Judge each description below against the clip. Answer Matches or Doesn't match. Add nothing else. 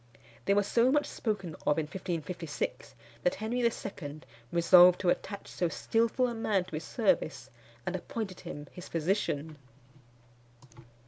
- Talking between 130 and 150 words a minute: Matches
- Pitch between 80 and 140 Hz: Doesn't match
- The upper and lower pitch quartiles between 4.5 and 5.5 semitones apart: Matches